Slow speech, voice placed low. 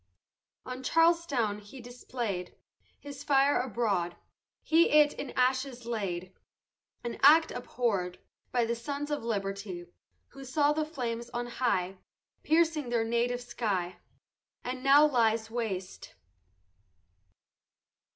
No: slow, 110 wpm; high, 240 Hz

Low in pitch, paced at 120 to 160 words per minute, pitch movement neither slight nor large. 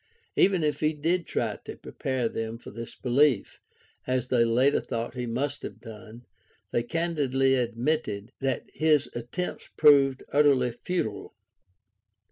Yes: low, 130 Hz; average, 145 wpm; average, 4.1 semitones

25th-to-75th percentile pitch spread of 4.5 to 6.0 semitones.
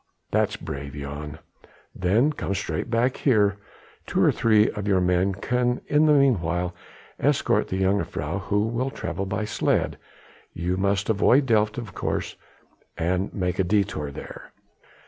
No: average, 4.1 semitones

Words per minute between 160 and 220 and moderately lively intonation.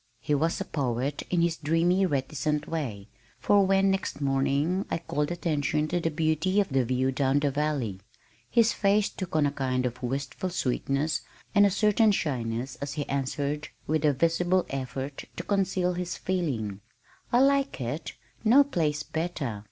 Yes: average, 165 wpm; average, 4.9 semitones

